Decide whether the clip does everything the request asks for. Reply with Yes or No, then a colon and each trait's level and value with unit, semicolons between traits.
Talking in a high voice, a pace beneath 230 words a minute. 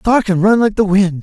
No: high, 200 Hz; fast, 295 wpm